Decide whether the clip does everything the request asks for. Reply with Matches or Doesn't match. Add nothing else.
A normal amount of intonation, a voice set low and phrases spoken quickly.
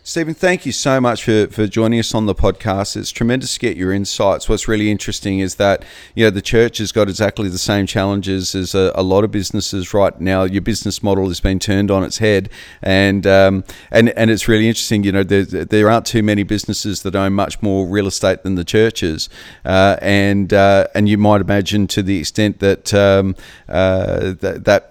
Doesn't match